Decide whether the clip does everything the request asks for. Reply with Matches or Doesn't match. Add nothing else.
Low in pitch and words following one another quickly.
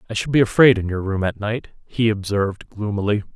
Matches